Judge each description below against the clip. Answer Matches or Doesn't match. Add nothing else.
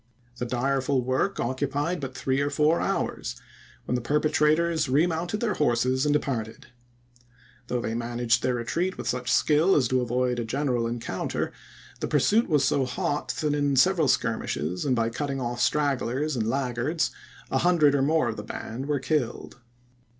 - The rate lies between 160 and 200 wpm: Matches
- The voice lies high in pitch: Doesn't match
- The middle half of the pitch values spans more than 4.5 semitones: Doesn't match